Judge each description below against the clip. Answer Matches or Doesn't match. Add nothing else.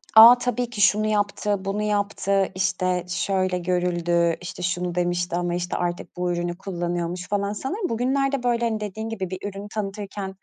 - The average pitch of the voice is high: Matches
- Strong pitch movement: Doesn't match